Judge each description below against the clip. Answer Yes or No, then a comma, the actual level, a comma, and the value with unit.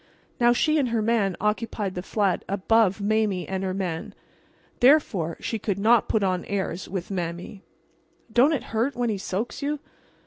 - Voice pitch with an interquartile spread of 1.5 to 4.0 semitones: Yes, average, 3.7 semitones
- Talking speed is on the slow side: No, average, 170 wpm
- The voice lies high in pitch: Yes, high, 205 Hz